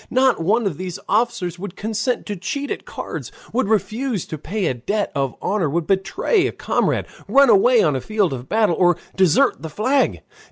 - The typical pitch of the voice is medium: No, high, 205 Hz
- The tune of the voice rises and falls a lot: Yes, wide, 5.8 semitones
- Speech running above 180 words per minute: Yes, average, 195 wpm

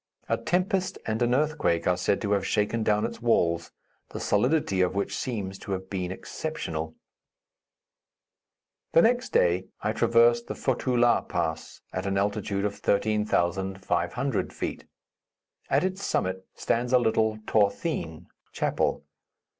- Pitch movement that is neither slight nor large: Yes, average, 4.4 semitones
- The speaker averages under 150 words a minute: Yes, average, 140 wpm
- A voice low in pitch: Yes, low, 105 Hz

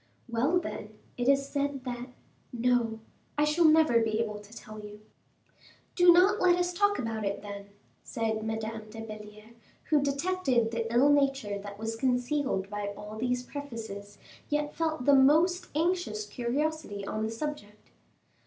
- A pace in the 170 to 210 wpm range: No, average, 155 wpm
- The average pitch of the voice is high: Yes, high, 240 Hz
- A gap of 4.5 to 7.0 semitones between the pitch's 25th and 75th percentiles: Yes, wide, 5.5 semitones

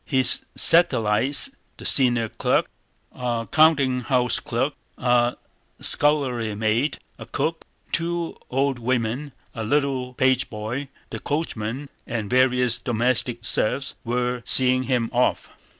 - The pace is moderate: No, slow, 105 wpm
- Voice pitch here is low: Yes, low, 125 Hz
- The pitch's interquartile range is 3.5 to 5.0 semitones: No, average, 2.9 semitones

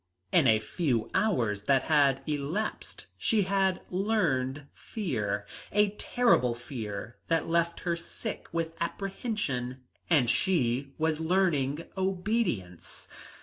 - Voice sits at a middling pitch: Yes, medium, 160 Hz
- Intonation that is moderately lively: No, wide, 7.1 semitones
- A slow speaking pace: Yes, slow, 110 wpm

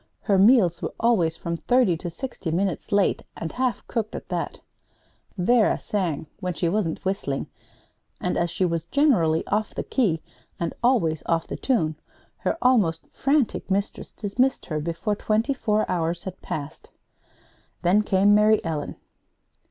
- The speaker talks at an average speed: Yes, average, 150 wpm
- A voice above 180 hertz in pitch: Yes, high, 190 Hz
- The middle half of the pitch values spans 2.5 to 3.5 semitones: No, average, 4.9 semitones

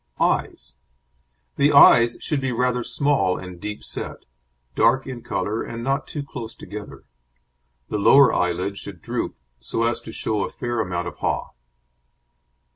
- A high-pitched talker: No, low, 115 Hz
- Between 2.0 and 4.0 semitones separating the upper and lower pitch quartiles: No, average, 4.9 semitones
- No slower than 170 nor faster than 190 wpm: No, average, 150 wpm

